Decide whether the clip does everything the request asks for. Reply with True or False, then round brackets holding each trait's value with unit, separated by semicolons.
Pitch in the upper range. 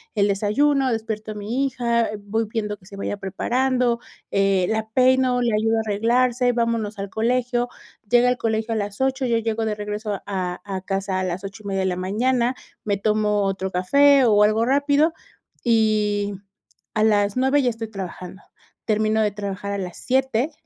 True (220 Hz)